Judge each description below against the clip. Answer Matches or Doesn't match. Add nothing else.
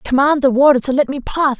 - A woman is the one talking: Matches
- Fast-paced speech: Matches